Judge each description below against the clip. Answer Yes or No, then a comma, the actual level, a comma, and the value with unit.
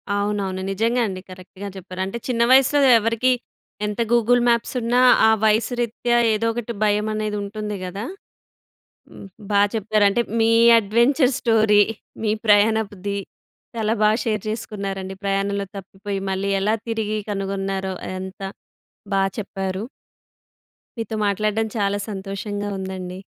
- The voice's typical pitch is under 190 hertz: No, high, 210 Hz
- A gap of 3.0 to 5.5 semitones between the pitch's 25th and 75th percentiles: No, narrow, 2.4 semitones